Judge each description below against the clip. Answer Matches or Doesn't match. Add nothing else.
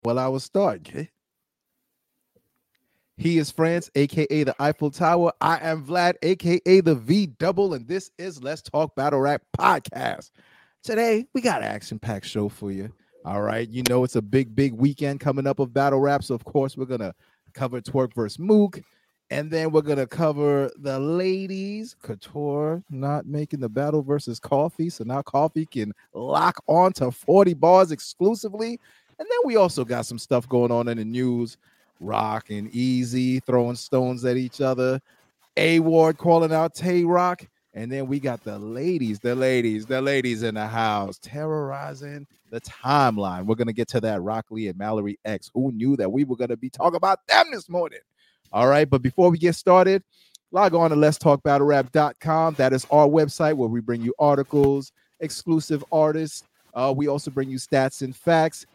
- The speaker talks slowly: Doesn't match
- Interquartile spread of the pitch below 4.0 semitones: Doesn't match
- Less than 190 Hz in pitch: Matches